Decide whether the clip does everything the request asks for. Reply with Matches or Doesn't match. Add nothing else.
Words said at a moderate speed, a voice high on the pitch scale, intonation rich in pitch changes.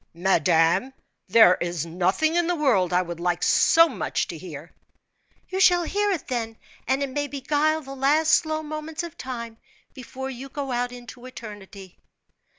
Matches